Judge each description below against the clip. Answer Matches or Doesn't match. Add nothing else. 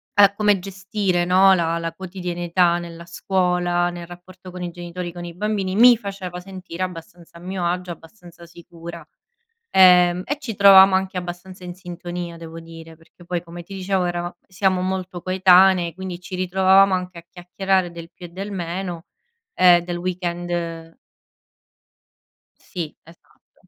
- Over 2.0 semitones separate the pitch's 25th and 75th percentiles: Doesn't match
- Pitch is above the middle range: Doesn't match